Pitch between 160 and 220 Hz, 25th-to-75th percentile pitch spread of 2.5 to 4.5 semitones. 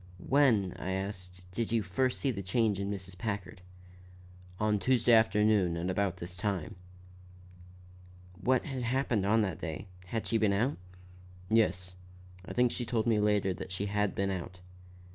No: low, 105 Hz; average, 3.6 semitones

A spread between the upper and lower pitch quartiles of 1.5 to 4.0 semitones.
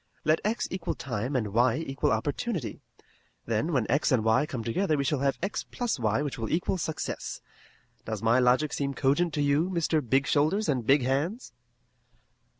No: average, 4.7 semitones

